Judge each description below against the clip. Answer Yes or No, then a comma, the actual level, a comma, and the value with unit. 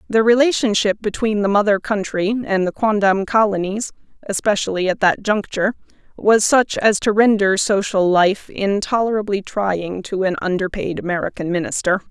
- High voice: Yes, high, 200 Hz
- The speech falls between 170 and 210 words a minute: No, average, 145 wpm